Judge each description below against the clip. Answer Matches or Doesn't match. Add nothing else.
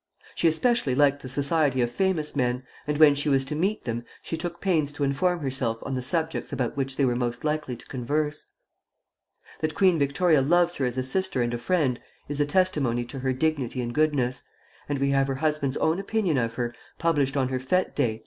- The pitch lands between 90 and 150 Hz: Matches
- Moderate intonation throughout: Matches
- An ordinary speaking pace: Doesn't match